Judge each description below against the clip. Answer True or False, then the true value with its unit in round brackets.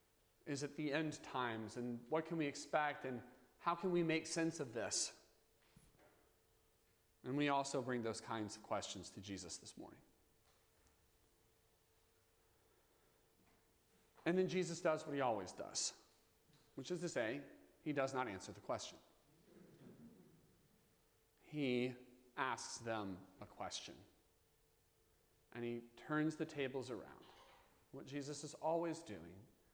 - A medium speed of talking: False (130 wpm)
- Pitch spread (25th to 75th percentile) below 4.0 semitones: False (5.5 semitones)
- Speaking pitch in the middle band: False (125 Hz)